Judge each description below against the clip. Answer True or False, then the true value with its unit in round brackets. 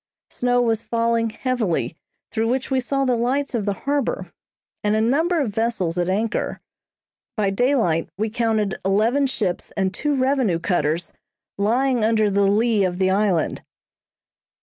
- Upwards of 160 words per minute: False (150 wpm)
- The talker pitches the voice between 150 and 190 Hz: False (225 Hz)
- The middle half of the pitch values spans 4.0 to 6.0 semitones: True (4.3 semitones)